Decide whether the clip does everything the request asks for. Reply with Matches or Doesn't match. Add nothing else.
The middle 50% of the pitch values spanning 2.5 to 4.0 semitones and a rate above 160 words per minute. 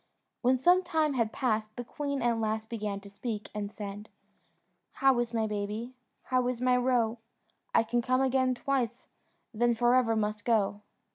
Matches